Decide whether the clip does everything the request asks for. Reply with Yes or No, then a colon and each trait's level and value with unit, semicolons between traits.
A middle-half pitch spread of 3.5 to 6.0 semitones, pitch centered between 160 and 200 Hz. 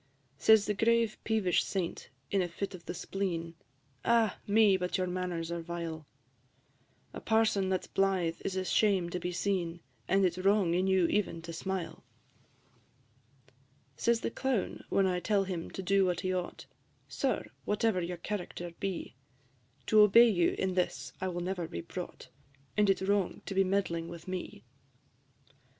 No: narrow, 2.6 semitones; medium, 185 Hz